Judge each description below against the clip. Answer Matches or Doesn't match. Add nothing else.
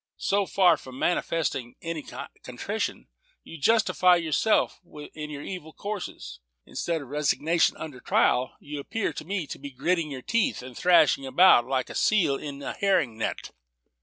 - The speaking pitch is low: Doesn't match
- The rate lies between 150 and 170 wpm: Matches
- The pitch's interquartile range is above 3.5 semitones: Matches